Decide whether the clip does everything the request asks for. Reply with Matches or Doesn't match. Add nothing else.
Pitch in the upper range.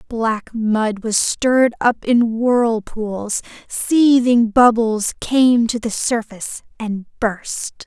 Matches